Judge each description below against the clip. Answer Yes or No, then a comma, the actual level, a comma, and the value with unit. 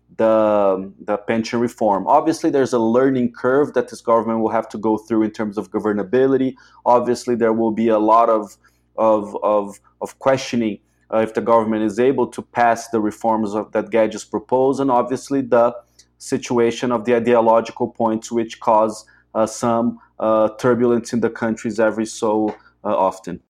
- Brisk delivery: No, average, 170 wpm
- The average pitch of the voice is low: Yes, low, 115 Hz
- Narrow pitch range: Yes, narrow, 1.9 semitones